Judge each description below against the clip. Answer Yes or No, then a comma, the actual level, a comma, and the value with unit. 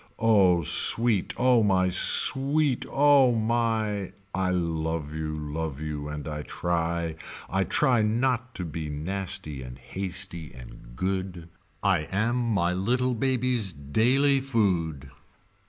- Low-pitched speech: Yes, very low, 95 Hz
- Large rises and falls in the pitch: Yes, wide, 6.6 semitones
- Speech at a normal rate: No, slow, 125 wpm